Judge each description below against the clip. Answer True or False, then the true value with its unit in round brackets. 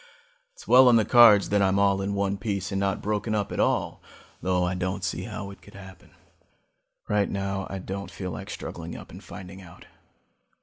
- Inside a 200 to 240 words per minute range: True (205 wpm)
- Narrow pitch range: True (1.4 semitones)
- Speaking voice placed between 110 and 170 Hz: False (100 Hz)